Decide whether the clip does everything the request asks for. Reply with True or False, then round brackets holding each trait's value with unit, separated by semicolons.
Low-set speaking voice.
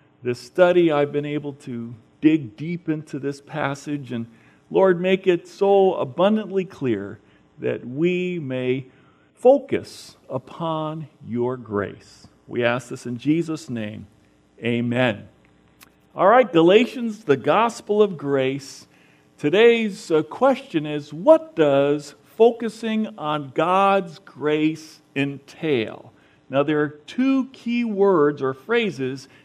False (150 Hz)